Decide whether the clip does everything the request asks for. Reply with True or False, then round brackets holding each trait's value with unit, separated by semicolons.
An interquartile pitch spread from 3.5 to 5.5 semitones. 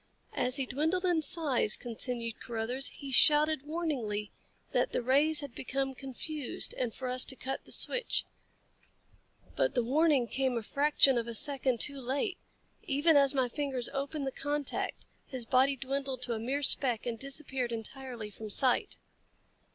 False (2.8 semitones)